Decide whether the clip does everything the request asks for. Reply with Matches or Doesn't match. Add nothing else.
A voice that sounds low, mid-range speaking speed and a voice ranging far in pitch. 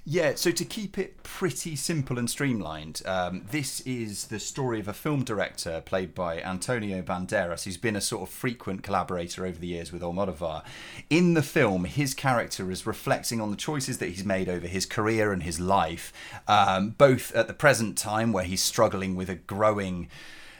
Matches